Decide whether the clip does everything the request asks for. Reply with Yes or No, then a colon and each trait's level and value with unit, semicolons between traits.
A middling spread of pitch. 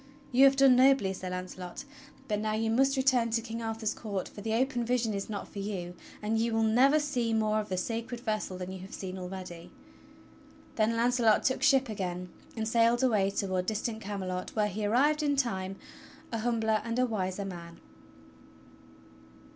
Yes: average, 3.9 semitones